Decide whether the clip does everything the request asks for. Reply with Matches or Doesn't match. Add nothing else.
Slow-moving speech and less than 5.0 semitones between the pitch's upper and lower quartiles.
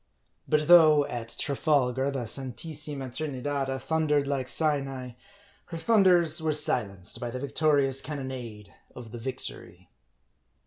Matches